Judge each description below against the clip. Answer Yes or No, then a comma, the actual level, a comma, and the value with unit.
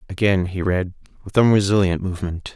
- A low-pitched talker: Yes, very low, 95 Hz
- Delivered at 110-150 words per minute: Yes, average, 140 wpm